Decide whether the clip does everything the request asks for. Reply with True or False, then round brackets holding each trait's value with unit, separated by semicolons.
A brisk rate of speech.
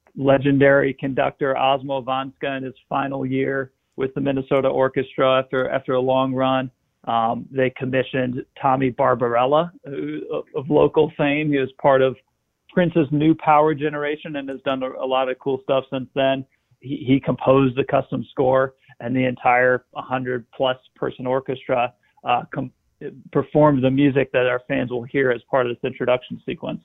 False (165 wpm)